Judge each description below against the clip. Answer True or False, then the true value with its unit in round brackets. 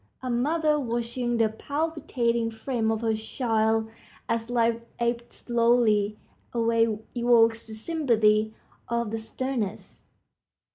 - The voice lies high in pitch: True (230 Hz)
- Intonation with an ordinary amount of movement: False (1.6 semitones)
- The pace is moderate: False (110 wpm)